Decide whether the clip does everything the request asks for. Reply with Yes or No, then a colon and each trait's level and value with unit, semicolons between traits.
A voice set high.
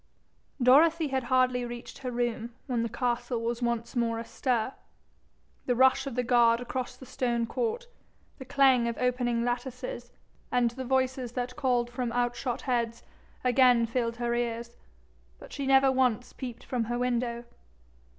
Yes: high, 245 Hz